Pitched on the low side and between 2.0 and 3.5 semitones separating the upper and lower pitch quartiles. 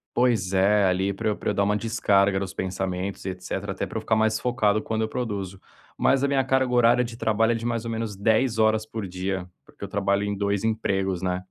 Yes: low, 105 Hz; average, 2.8 semitones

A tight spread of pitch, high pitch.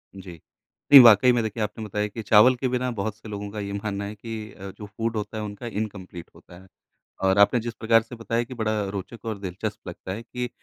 No: narrow, 2.3 semitones; low, 110 Hz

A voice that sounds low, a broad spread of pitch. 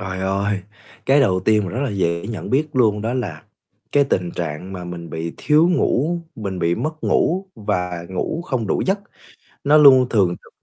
Yes: low, 105 Hz; wide, 7.3 semitones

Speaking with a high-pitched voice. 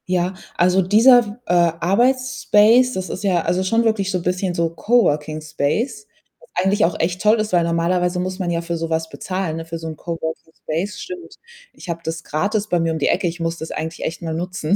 No: medium, 180 Hz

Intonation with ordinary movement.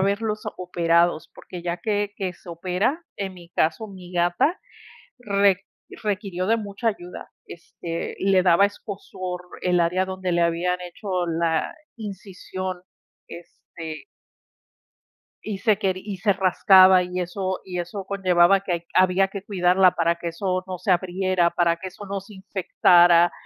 No: narrow, 2.1 semitones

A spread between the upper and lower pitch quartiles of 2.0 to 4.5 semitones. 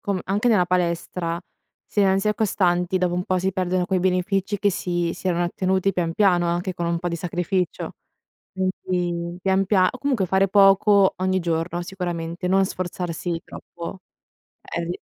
No: narrow, 1.6 semitones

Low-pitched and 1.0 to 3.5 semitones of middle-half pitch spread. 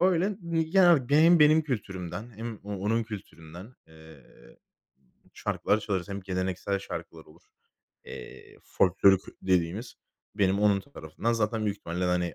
No: low, 100 Hz; average, 4.8 semitones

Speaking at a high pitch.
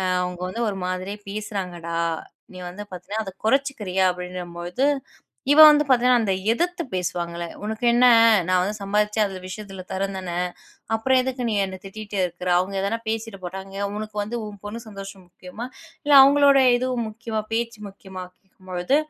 Yes: high, 200 Hz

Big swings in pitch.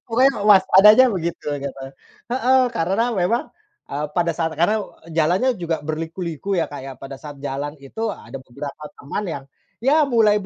Yes: wide, 6.9 semitones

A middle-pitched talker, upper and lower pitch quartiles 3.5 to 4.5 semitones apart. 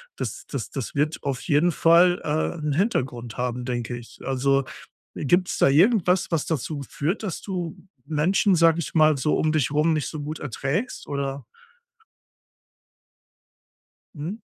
Yes: medium, 150 Hz; average, 3.9 semitones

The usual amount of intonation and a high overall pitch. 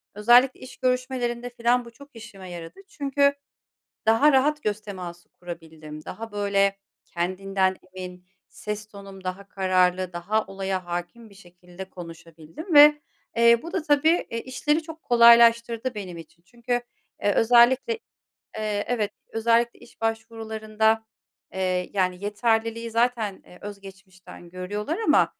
Yes: average, 4.3 semitones; high, 215 Hz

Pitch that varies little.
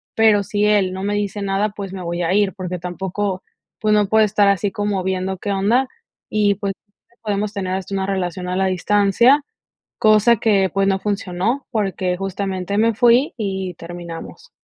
Yes: narrow, 1.9 semitones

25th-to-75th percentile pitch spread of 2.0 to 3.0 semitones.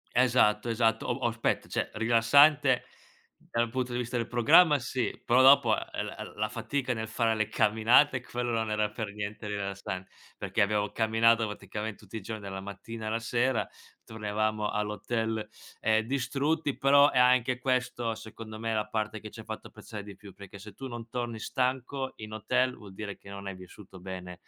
Yes: narrow, 2.6 semitones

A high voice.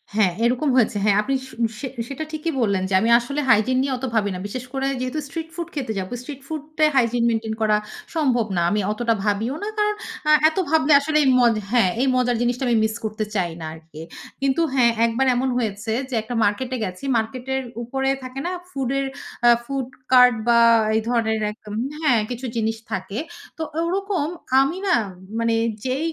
Yes: very high, 250 Hz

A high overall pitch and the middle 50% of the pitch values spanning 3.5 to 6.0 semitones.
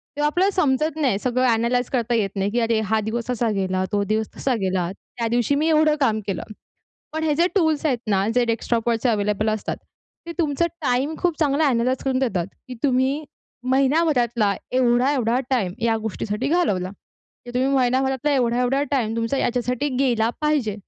Yes: high, 245 Hz; average, 4.0 semitones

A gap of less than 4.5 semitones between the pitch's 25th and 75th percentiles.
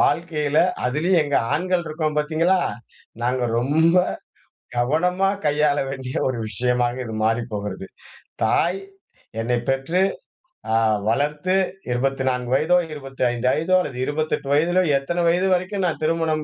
No: average, 4.8 semitones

